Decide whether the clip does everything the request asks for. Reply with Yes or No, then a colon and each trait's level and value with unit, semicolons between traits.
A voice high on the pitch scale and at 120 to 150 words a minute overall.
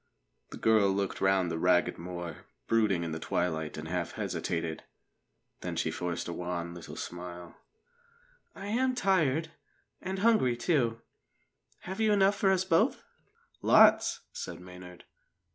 No: very low, 95 Hz; average, 140 wpm